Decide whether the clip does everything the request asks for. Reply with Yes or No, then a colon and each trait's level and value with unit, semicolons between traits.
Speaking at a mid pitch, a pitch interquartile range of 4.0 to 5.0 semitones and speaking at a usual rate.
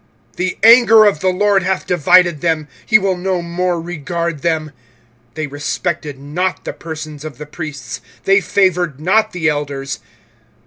No: medium, 170 Hz; average, 3.5 semitones; average, 155 wpm